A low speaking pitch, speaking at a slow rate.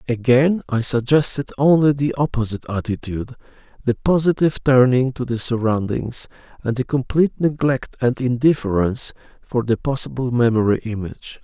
Yes: low, 125 Hz; slow, 125 wpm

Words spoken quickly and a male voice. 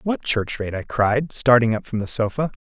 Yes: fast, 230 wpm; male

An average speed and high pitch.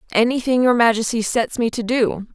Yes: average, 180 wpm; high, 230 Hz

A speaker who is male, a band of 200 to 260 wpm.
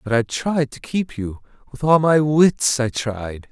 Yes: male; fast, 205 wpm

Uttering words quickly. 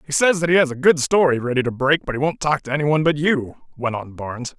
Yes: fast, 290 wpm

